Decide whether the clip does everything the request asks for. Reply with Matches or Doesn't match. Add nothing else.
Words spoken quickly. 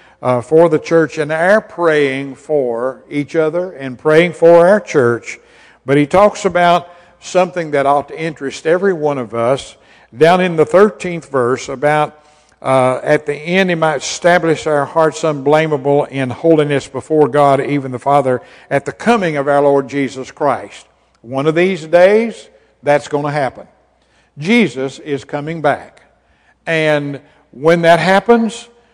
Doesn't match